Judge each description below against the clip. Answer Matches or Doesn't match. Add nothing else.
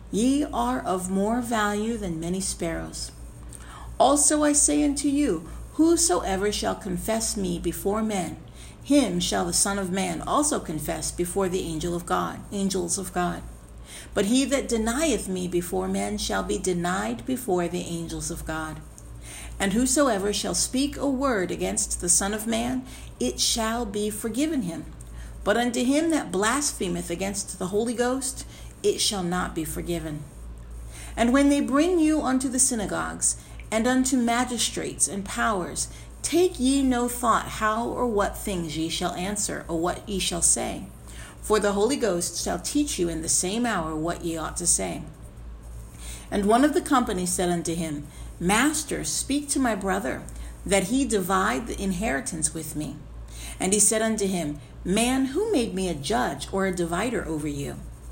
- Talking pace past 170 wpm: Doesn't match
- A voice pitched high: Matches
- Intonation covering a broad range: Matches